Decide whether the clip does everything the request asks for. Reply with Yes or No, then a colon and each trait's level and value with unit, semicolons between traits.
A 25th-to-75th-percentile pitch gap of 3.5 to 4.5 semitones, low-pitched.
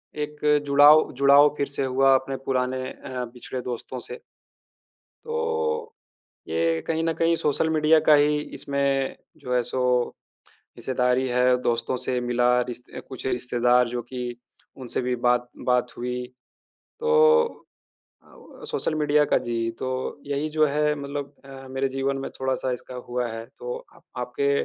No: average, 2.8 semitones; low, 130 Hz